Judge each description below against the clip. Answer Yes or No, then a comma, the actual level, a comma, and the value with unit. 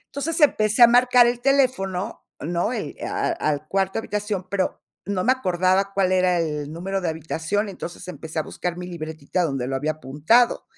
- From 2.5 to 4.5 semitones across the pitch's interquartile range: No, average, 5.0 semitones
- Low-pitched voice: No, medium, 185 Hz